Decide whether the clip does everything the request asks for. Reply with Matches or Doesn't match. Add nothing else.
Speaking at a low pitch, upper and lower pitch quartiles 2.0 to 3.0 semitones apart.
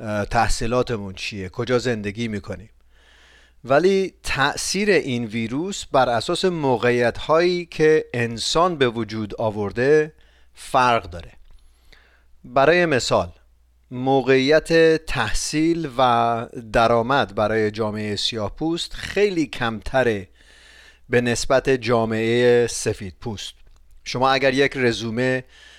Doesn't match